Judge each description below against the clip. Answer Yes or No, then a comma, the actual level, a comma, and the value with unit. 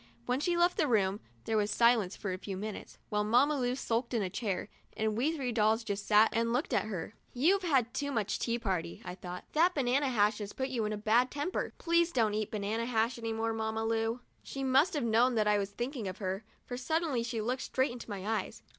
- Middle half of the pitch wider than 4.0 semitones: No, average, 3.5 semitones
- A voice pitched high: Yes, high, 230 Hz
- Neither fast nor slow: No, fast, 235 wpm